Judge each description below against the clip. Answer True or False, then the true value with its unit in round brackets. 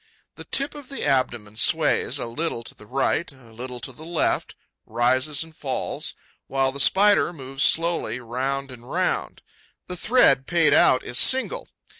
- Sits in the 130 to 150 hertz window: True (135 Hz)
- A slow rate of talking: False (165 wpm)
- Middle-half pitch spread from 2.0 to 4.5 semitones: False (5.0 semitones)